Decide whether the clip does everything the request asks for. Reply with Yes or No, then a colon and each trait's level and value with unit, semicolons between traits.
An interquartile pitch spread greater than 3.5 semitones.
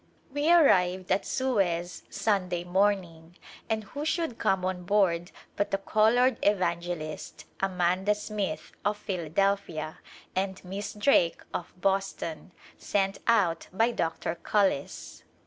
No: average, 3.1 semitones